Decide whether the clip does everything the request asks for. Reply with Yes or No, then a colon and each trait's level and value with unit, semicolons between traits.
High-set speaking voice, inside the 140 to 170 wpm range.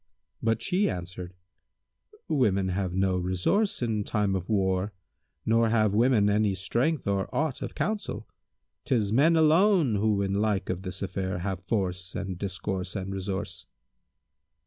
No: low, 100 Hz; average, 145 wpm